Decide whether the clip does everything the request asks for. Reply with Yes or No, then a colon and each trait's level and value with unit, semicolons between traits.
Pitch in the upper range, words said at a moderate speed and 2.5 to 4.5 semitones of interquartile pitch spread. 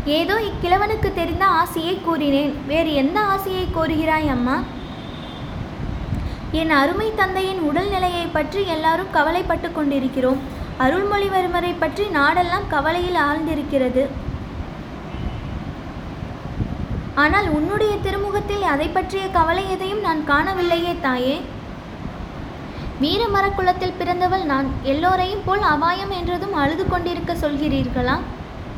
Yes: very high, 340 Hz; average, 90 wpm; average, 4.0 semitones